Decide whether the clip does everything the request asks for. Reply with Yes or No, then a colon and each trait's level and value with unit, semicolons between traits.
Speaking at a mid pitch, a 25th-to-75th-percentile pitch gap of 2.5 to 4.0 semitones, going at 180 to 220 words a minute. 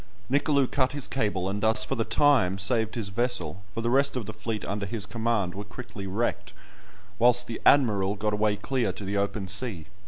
No: low, 110 Hz; average, 3.7 semitones; fast, 205 wpm